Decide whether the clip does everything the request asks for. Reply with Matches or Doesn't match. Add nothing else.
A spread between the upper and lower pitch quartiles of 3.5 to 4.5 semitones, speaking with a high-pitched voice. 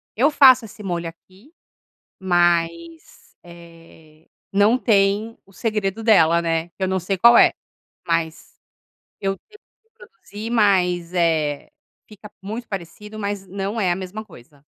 Matches